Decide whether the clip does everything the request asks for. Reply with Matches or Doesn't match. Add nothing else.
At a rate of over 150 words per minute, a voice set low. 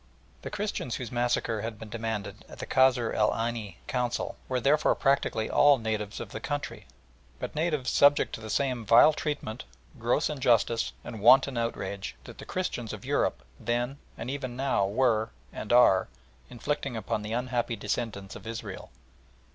Matches